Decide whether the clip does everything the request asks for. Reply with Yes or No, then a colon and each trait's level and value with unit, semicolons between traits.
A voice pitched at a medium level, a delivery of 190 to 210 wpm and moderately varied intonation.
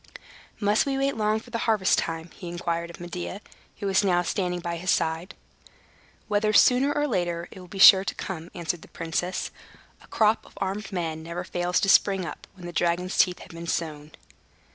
Yes: medium, 180 Hz; average, 195 wpm; average, 3.3 semitones